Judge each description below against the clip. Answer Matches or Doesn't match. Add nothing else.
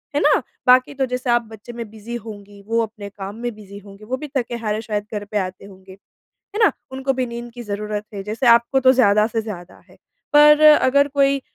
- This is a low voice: Doesn't match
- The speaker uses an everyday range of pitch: Matches